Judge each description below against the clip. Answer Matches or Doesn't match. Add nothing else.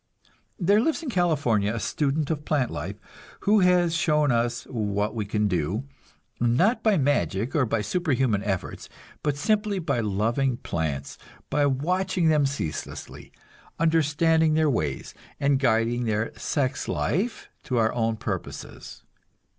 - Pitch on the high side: Doesn't match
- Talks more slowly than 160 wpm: Matches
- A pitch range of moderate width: Doesn't match